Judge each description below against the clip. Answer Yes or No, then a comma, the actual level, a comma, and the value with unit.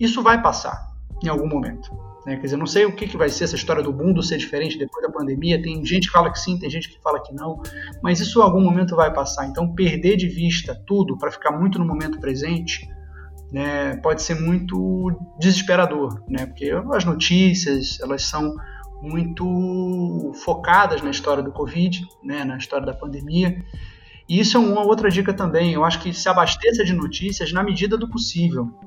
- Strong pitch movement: No, average, 4.2 semitones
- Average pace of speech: No, fast, 195 wpm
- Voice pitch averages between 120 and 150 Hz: No, medium, 170 Hz